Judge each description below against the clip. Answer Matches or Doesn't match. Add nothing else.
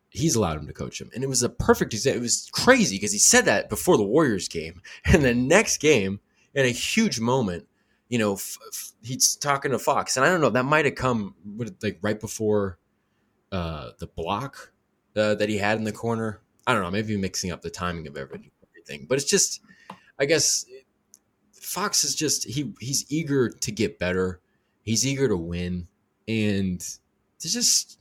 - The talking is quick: Doesn't match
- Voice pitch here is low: Matches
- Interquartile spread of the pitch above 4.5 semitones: Matches